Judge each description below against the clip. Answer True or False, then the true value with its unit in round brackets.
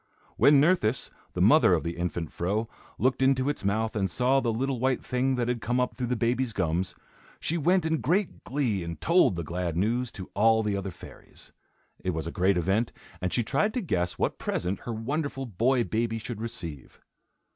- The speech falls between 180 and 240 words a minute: True (200 wpm)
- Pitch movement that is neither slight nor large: False (5.8 semitones)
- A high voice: False (115 Hz)